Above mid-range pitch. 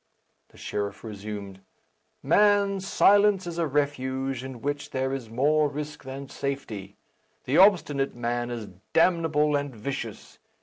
No: medium, 140 Hz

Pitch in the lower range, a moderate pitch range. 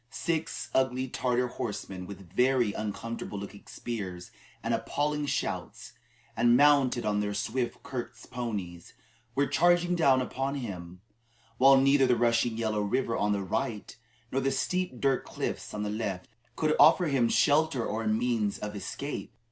Yes: low, 120 Hz; average, 4.6 semitones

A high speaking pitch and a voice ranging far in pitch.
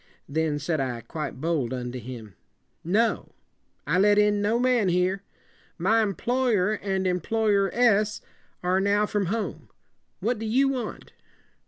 No: high, 200 Hz; average, 5.0 semitones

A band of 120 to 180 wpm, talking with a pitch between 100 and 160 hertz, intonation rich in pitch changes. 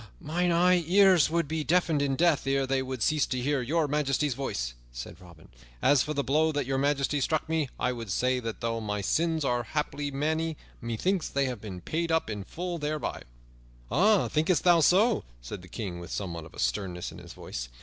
No: average, 200 wpm; medium, 140 Hz; wide, 5.9 semitones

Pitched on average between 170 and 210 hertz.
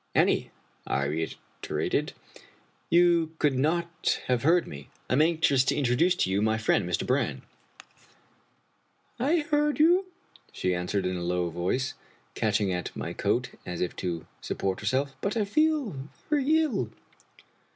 No: low, 135 Hz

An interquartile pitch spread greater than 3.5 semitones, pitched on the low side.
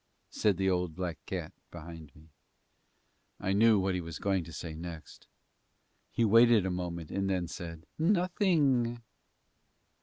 Yes: average, 5.3 semitones; very low, 95 Hz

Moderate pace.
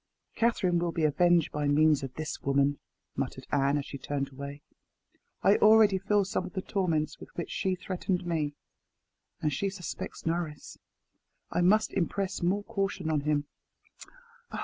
Yes: average, 155 wpm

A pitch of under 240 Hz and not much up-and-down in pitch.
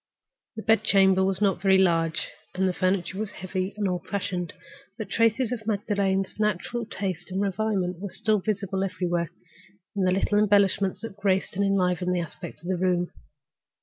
Yes: high, 190 Hz; narrow, 2.2 semitones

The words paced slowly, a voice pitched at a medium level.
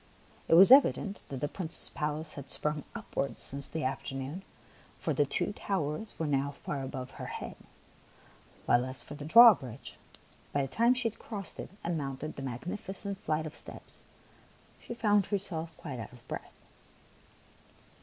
No: average, 165 wpm; medium, 155 Hz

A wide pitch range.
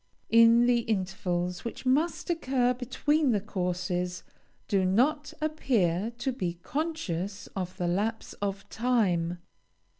Yes: wide, 5.9 semitones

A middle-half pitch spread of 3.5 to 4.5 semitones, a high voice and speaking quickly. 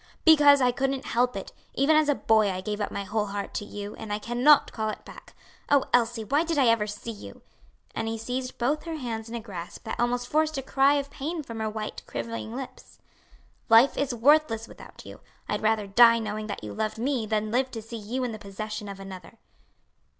Yes: average, 3.9 semitones; high, 230 Hz; fast, 225 wpm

